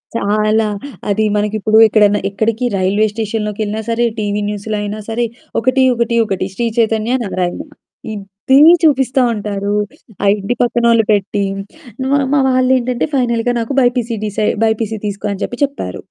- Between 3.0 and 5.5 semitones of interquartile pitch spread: No, narrow, 2.5 semitones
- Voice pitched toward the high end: Yes, high, 220 Hz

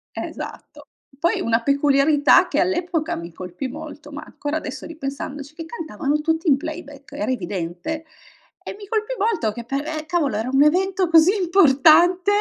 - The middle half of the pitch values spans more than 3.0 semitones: Yes, average, 3.7 semitones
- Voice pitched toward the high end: Yes, very high, 300 Hz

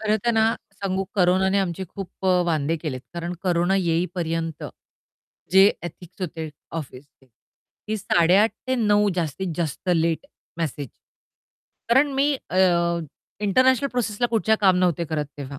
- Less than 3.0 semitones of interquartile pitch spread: No, average, 4.2 semitones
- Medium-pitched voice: Yes, medium, 180 Hz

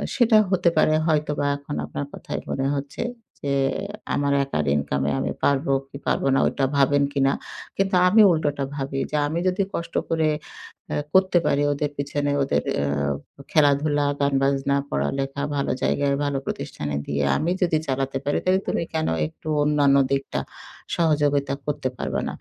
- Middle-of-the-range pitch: Yes, medium, 145 Hz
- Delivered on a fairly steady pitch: Yes, narrow, 2.2 semitones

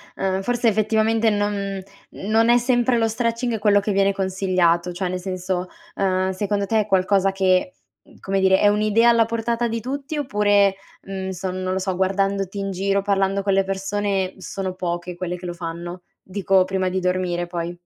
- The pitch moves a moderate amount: No, narrow, 2.3 semitones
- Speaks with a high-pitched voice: Yes, high, 195 Hz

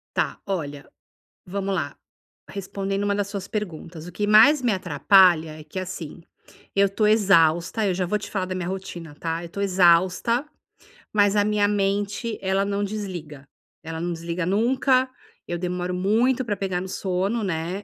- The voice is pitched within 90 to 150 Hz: No, high, 190 Hz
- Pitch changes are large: No, average, 2.8 semitones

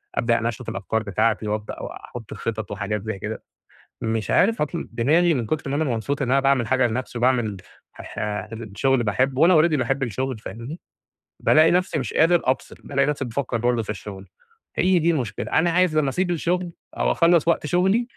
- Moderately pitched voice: No, low, 130 Hz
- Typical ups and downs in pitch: No, wide, 6.2 semitones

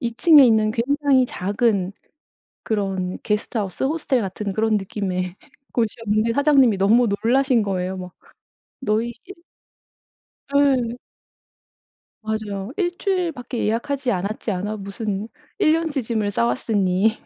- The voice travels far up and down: No, average, 4.5 semitones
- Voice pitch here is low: No, high, 220 Hz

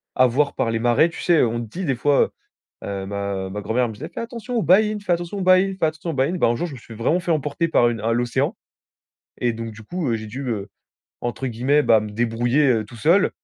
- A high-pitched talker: No, low, 125 Hz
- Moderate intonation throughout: No, wide, 6.8 semitones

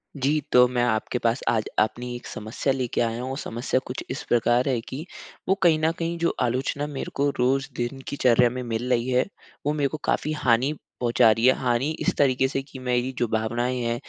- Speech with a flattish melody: Yes, narrow, 2.3 semitones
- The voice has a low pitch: Yes, low, 125 Hz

